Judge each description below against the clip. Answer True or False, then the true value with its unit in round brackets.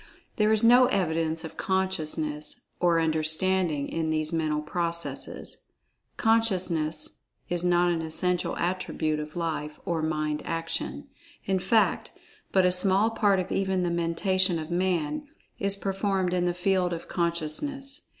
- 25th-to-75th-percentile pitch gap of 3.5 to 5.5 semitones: False (3.0 semitones)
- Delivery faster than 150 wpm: False (140 wpm)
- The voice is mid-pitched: True (175 Hz)